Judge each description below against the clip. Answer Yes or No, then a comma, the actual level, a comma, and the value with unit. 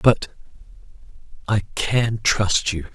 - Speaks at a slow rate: Yes, slow, 80 wpm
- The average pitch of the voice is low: Yes, low, 105 Hz